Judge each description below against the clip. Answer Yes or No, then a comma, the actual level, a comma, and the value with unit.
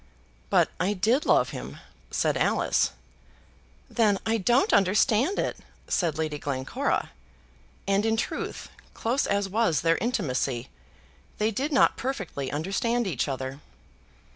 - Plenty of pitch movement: Yes, wide, 6.9 semitones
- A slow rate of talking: Yes, slow, 125 wpm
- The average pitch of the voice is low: No, high, 200 Hz